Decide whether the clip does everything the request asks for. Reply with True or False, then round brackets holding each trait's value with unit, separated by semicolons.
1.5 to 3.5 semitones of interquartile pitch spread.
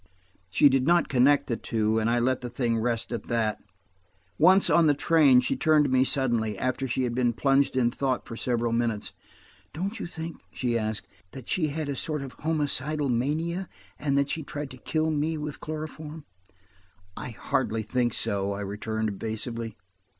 False (4.6 semitones)